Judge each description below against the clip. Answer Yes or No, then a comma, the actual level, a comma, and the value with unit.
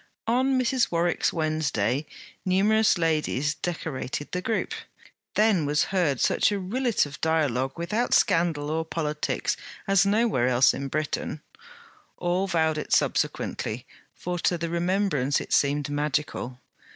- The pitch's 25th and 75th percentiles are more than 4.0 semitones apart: Yes, average, 4.9 semitones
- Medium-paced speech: No, slow, 130 wpm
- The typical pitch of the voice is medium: Yes, medium, 165 Hz